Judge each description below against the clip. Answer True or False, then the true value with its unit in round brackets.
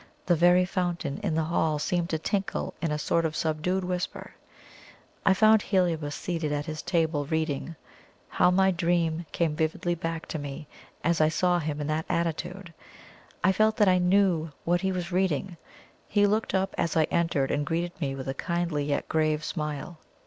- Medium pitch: True (170 Hz)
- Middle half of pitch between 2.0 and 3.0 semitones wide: True (2.7 semitones)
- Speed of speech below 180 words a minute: False (185 wpm)